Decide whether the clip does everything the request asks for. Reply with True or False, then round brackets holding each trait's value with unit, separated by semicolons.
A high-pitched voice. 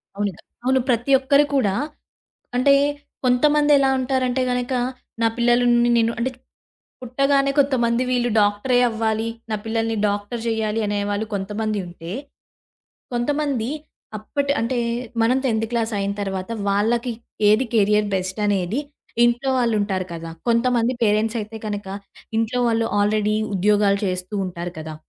True (225 Hz)